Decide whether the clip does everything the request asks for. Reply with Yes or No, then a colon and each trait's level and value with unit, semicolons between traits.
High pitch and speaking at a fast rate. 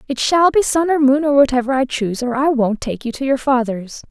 Yes: very high, 265 Hz; fast, 265 wpm